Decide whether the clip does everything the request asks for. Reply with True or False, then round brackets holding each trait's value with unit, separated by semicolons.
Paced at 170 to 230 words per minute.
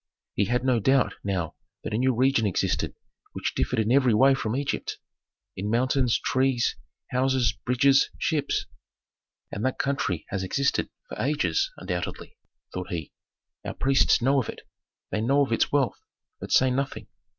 False (160 wpm)